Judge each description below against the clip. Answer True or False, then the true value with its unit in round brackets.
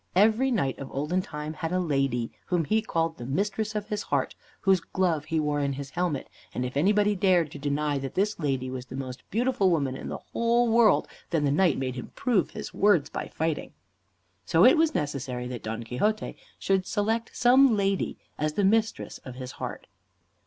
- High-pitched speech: False (165 Hz)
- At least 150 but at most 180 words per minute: False (200 wpm)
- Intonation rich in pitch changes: True (7.0 semitones)